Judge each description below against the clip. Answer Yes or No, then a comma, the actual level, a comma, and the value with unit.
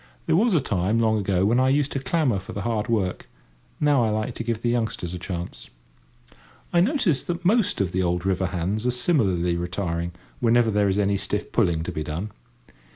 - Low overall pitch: Yes, low, 105 Hz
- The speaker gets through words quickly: Yes, fast, 210 wpm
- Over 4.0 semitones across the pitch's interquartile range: Yes, wide, 5.5 semitones